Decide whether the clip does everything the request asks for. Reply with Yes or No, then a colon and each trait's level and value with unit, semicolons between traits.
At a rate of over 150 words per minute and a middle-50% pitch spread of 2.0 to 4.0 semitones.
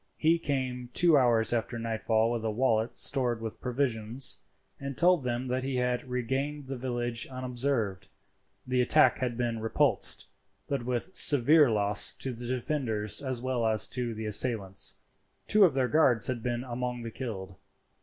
Yes: average, 165 wpm; narrow, 2.5 semitones